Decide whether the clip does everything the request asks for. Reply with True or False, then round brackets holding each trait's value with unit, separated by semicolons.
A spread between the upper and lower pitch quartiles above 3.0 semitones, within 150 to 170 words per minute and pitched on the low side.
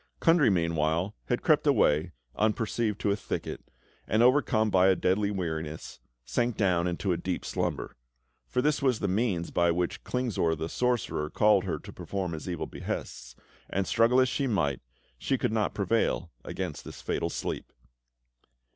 True (5.2 semitones; 165 wpm; 95 Hz)